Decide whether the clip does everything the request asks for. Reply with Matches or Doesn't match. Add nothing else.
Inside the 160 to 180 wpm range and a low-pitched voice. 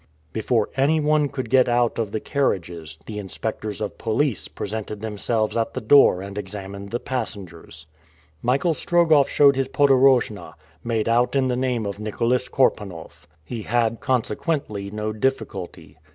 Doesn't match